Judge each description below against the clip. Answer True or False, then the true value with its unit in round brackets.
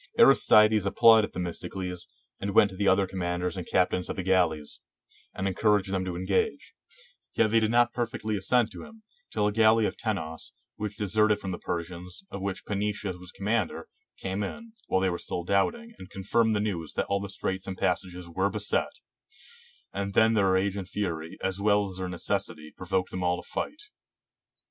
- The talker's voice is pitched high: False (95 Hz)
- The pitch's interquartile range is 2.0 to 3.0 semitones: True (2.7 semitones)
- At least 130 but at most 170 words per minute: False (190 wpm)